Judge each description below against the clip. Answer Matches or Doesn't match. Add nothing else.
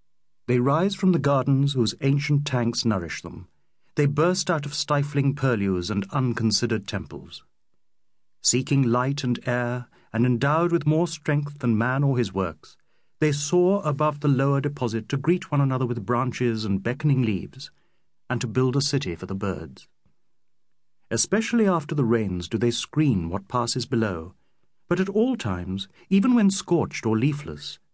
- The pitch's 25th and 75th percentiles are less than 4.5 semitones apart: Doesn't match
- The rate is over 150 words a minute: Matches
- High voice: Doesn't match